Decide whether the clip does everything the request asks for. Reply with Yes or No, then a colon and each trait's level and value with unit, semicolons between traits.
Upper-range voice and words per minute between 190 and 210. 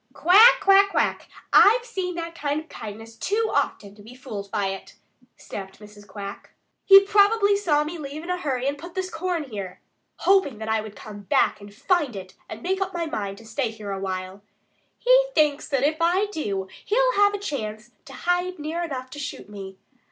Yes: very high, 290 Hz; fast, 205 wpm